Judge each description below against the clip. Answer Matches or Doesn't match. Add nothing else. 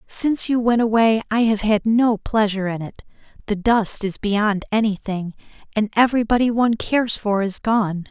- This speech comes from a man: Doesn't match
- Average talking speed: Matches